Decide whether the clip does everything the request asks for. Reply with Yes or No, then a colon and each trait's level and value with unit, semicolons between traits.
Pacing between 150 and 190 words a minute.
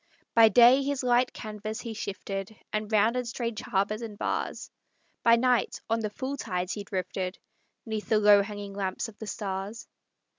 Yes: average, 170 wpm